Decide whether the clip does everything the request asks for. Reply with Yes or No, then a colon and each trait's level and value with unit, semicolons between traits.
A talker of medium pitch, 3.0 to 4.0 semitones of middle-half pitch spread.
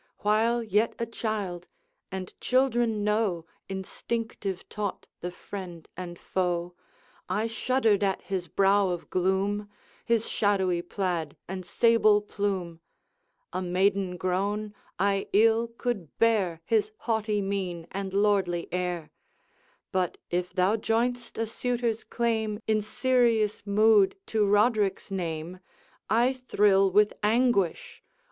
No: high, 205 Hz; average, 3.3 semitones